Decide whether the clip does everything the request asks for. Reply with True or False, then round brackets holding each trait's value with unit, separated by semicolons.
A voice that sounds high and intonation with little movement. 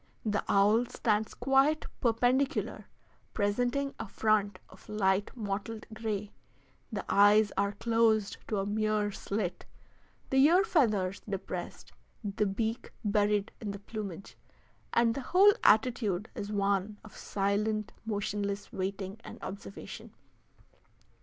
True (210 Hz; 2.1 semitones)